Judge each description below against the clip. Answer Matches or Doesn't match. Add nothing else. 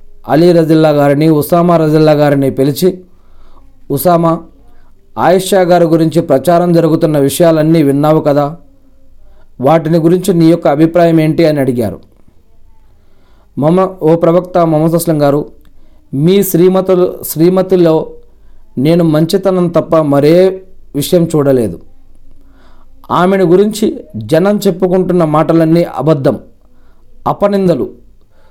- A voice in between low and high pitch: Matches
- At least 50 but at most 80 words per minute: Doesn't match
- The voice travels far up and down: Matches